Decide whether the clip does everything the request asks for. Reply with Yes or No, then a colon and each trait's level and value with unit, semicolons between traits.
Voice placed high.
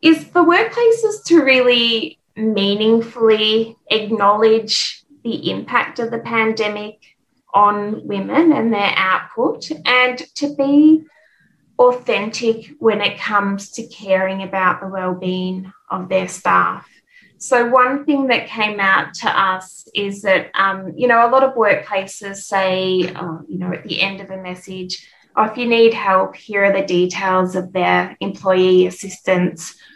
Yes: high, 210 Hz